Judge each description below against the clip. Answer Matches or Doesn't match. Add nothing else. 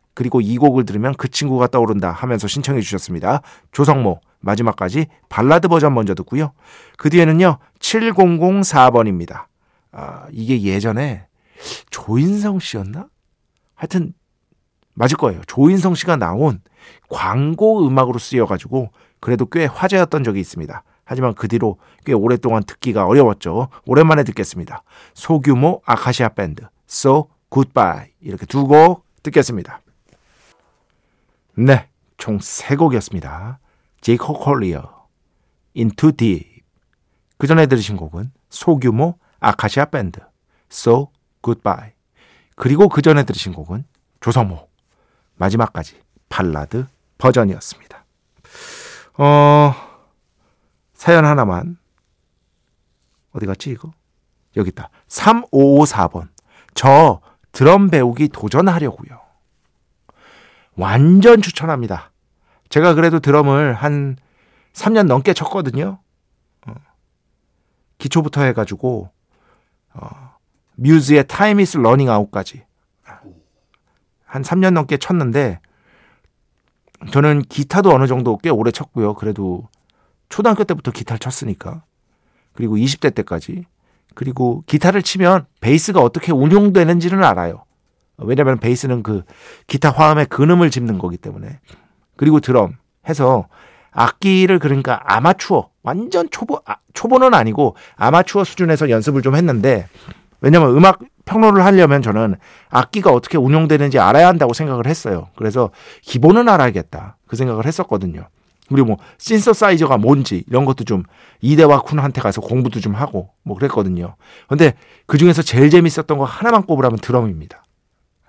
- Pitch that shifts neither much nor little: Doesn't match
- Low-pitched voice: Matches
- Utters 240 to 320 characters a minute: Matches